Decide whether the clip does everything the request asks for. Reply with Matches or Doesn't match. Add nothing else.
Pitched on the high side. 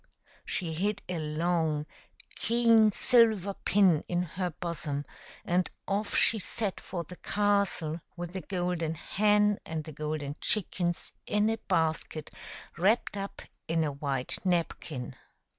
Doesn't match